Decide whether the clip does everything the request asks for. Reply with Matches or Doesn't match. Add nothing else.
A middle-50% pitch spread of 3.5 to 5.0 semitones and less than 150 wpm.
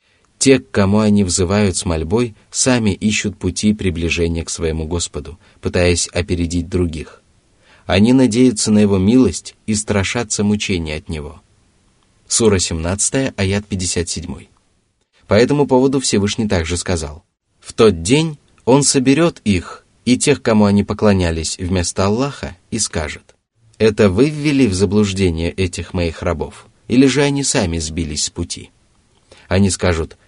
Matches